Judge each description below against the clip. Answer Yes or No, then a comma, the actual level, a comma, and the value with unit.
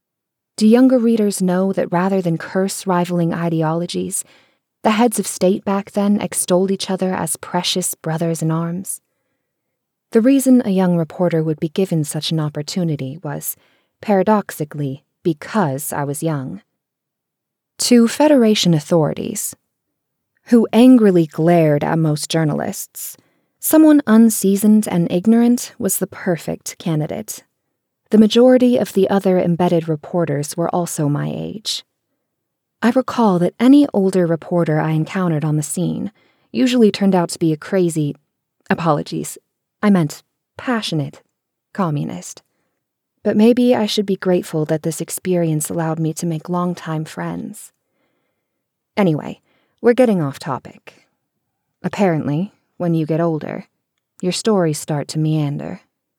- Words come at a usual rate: No, slow, 130 wpm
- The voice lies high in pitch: No, medium, 180 Hz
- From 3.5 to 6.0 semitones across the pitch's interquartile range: Yes, average, 4.5 semitones